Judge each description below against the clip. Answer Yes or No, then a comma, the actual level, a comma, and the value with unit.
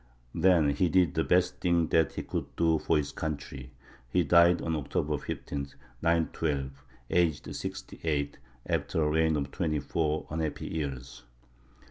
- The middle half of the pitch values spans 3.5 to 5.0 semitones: No, average, 2.8 semitones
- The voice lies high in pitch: No, very low, 80 Hz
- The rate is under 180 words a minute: Yes, average, 150 wpm